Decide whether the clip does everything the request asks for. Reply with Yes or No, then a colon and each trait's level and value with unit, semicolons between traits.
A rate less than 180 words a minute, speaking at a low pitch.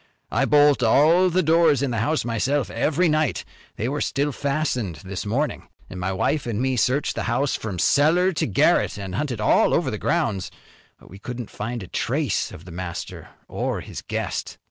No: average, 185 wpm; low, 130 Hz